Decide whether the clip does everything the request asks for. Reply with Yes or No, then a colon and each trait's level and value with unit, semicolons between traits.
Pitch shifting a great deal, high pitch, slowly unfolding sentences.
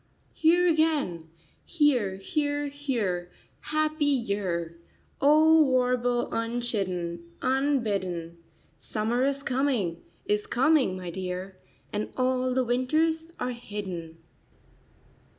Yes: wide, 7.4 semitones; high, 245 Hz; slow, 95 wpm